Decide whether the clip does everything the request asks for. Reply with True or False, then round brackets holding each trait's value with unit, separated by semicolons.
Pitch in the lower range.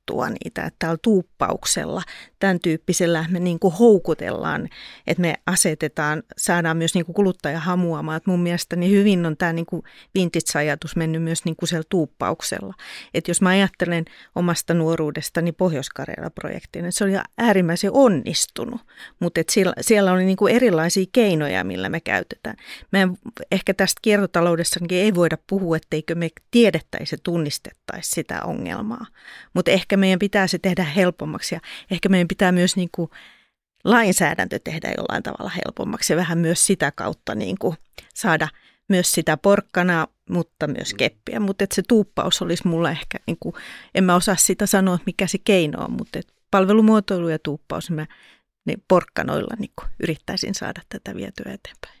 False (180 Hz)